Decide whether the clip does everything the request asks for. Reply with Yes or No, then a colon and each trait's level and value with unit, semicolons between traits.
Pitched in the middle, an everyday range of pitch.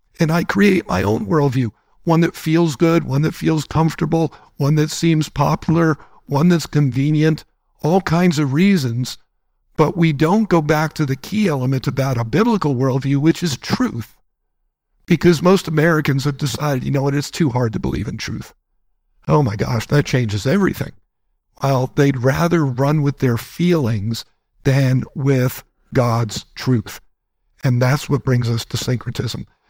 Yes: medium, 145 Hz; average, 3.9 semitones